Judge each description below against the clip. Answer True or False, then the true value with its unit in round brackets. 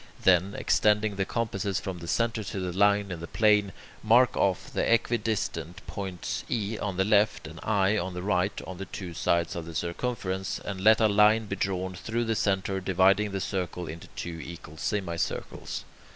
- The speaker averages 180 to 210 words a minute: True (185 wpm)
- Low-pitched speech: True (95 Hz)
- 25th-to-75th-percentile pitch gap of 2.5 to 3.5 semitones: True (2.8 semitones)